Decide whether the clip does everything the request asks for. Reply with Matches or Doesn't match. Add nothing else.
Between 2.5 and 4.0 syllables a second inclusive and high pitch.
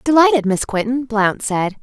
Doesn't match